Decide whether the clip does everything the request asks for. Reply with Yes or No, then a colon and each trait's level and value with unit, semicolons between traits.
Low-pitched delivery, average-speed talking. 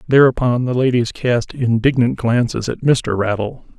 Yes: low, 120 Hz; average, 145 wpm